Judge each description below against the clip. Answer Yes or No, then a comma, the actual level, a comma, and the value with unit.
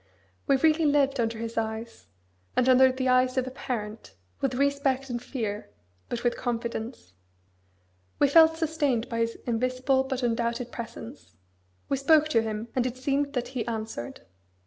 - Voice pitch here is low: No, very high, 250 Hz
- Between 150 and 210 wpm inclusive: Yes, average, 160 wpm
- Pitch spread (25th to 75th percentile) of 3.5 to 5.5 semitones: No, average, 3.0 semitones